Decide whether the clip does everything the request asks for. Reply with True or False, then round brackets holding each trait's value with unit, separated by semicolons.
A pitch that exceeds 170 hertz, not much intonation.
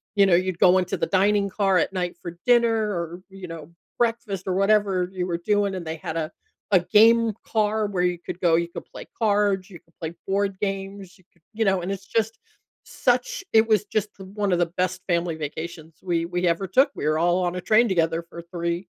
False (185 Hz; 3.0 semitones)